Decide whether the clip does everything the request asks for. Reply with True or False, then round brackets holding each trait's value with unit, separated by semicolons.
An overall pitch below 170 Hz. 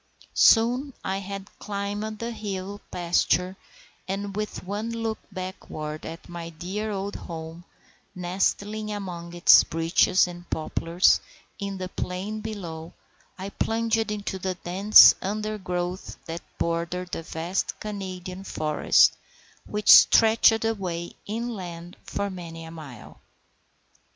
False (190 Hz)